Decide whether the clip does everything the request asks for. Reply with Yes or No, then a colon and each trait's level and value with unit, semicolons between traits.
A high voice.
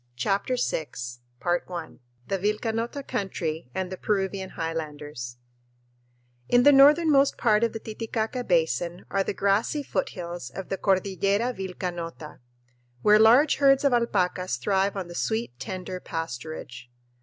Yes: high, 195 Hz